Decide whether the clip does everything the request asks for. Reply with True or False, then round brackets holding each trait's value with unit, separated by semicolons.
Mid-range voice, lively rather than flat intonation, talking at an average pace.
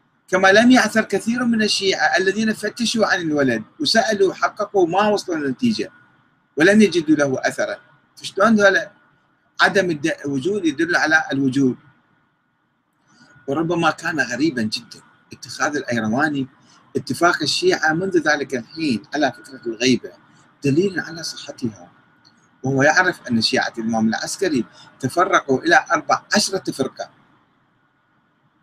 True (175 Hz; 7.2 semitones; 115 wpm)